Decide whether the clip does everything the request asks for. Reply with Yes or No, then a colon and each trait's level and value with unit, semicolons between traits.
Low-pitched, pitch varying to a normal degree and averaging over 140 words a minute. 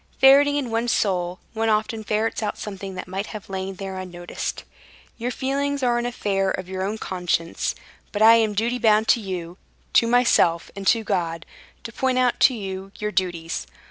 No: high, 210 Hz; average, 3.9 semitones; average, 190 wpm